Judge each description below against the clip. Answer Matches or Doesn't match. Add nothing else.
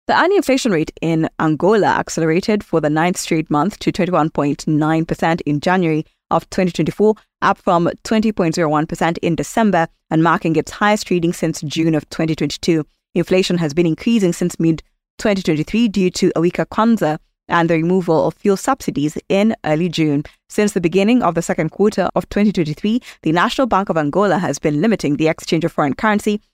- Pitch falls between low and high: Matches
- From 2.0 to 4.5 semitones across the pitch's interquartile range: Matches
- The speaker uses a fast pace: Doesn't match